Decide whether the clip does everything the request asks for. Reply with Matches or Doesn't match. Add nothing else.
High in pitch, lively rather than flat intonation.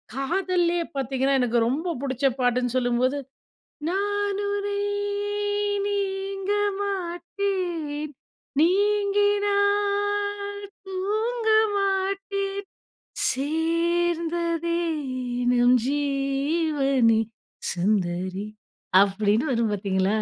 Matches